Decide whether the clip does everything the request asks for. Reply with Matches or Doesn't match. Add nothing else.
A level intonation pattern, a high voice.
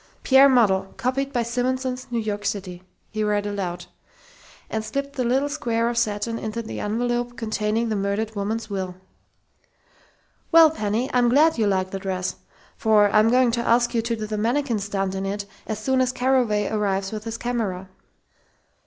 Doesn't match